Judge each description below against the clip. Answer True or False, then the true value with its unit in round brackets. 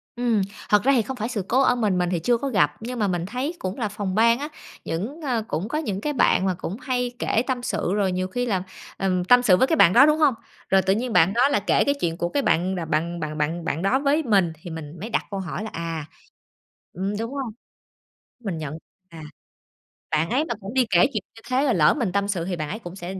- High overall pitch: True (205 Hz)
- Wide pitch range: True (5.8 semitones)